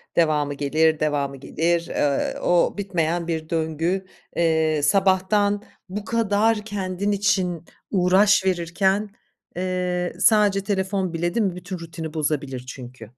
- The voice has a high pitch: No, medium, 175 Hz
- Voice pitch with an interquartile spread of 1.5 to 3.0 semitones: No, average, 3.7 semitones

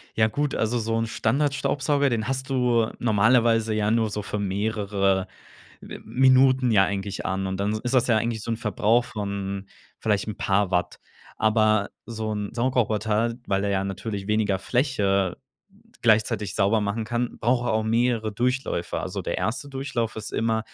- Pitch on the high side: No, low, 110 Hz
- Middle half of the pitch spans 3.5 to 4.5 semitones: No, average, 2.9 semitones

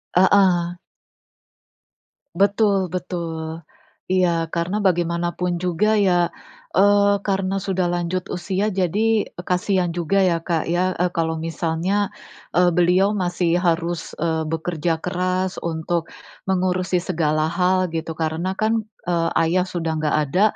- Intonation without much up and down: Yes, narrow, 2.1 semitones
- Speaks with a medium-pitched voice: Yes, medium, 180 Hz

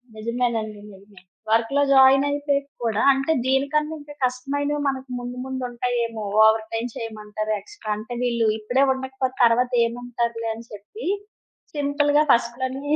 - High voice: Yes, high, 245 Hz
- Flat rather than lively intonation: No, average, 3.3 semitones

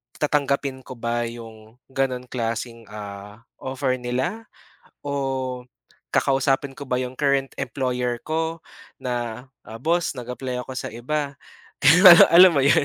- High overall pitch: No, low, 130 Hz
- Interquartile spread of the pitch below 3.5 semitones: Yes, narrow, 2.6 semitones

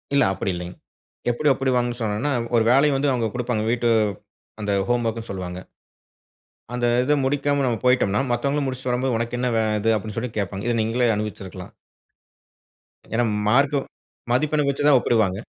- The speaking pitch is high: No, low, 120 Hz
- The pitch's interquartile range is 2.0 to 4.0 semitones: Yes, average, 3.6 semitones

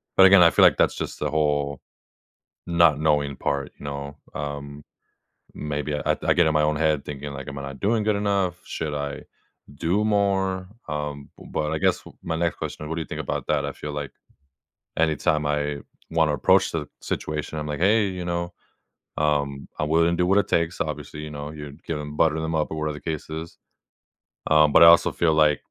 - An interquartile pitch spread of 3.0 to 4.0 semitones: No, narrow, 2.4 semitones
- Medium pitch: No, very low, 75 Hz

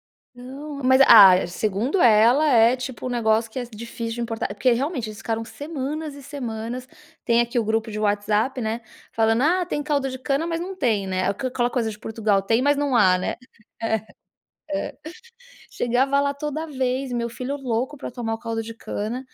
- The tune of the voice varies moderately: Yes, average, 3.6 semitones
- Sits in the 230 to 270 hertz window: Yes, high, 240 Hz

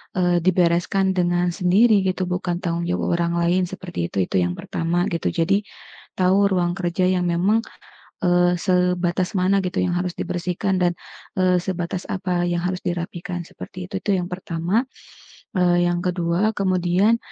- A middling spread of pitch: No, narrow, 1.2 semitones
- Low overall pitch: No, medium, 180 Hz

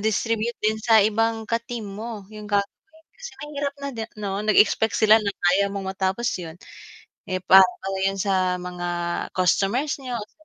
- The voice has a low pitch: No, high, 210 Hz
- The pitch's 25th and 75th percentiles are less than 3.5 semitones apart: Yes, average, 3.1 semitones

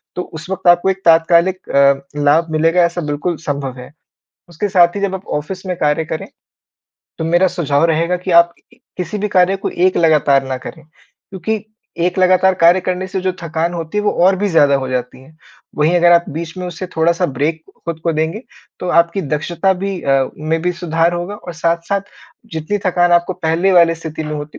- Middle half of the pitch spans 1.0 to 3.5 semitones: Yes, narrow, 2.6 semitones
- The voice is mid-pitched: Yes, medium, 170 Hz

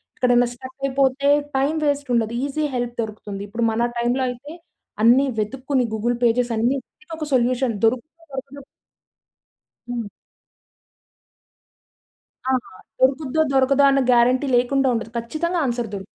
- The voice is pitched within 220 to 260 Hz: Yes, very high, 250 Hz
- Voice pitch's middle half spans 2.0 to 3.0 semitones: Yes, narrow, 2.6 semitones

